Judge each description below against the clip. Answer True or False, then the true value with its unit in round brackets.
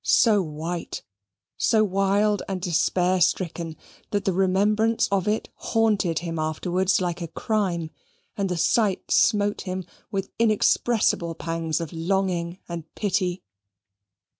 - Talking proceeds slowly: True (125 wpm)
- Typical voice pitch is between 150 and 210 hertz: True (185 Hz)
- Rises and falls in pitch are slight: False (3.2 semitones)